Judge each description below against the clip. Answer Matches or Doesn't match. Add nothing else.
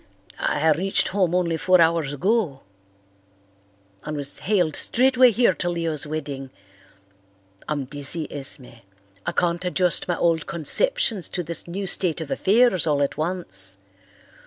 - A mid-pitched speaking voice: Matches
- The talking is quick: Doesn't match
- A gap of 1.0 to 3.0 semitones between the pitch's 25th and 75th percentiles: Doesn't match